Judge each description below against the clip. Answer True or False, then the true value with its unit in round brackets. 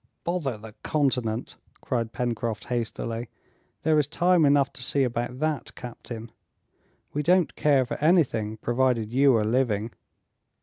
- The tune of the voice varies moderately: True (4.0 semitones)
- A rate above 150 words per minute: False (135 wpm)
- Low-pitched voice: True (125 Hz)